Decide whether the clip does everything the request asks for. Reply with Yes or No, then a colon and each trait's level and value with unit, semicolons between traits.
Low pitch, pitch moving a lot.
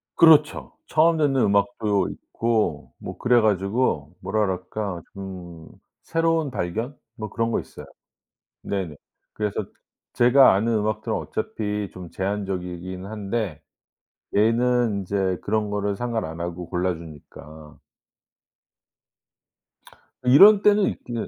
No: low, 105 Hz; average, 4.6 semitones